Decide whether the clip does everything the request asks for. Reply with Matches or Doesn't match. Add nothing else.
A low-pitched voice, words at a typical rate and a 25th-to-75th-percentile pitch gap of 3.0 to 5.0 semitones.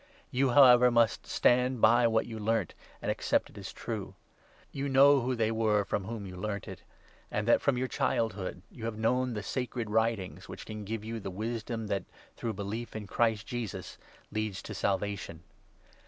Doesn't match